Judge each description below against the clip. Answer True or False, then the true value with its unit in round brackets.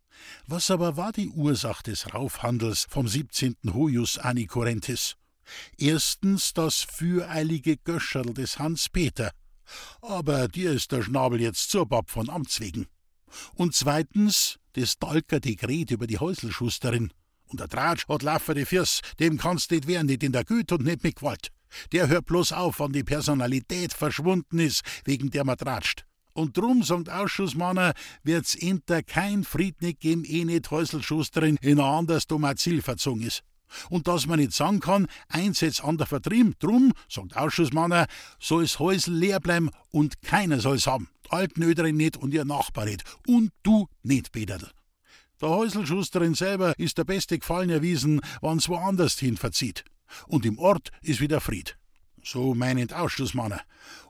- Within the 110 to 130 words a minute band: False (155 wpm)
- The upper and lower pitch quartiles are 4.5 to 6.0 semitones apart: True (4.8 semitones)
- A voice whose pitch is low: False (155 Hz)